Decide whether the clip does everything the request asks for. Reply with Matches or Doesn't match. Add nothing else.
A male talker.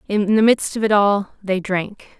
Doesn't match